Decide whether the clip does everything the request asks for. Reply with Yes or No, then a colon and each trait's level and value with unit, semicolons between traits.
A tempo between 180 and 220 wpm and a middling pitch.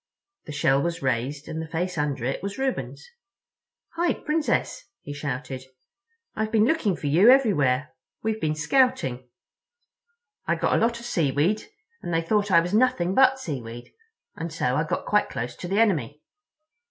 No: average, 165 wpm; medium, 165 Hz